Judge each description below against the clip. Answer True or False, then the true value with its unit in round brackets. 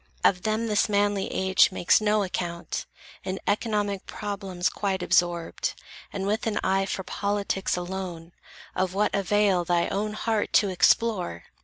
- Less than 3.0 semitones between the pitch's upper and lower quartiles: True (2.4 semitones)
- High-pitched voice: True (195 Hz)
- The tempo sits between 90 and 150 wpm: True (145 wpm)